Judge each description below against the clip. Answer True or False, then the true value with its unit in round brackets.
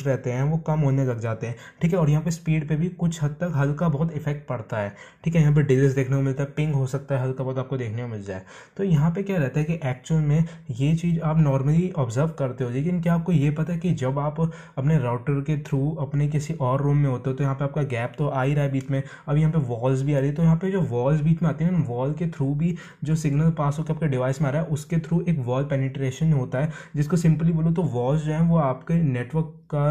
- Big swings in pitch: False (3.2 semitones)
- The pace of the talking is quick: True (210 wpm)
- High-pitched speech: False (150 Hz)